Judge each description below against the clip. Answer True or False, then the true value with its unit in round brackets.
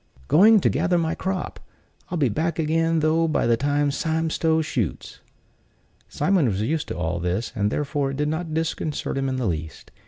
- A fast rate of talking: False (195 wpm)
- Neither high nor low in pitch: True (150 Hz)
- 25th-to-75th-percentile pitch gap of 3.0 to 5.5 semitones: True (4.8 semitones)